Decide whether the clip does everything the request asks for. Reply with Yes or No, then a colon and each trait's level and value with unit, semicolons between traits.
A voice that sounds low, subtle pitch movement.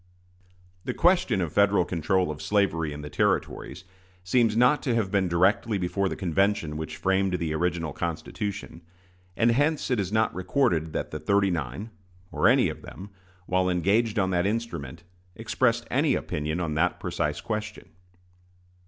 No: very low, 95 Hz; average, 4.2 semitones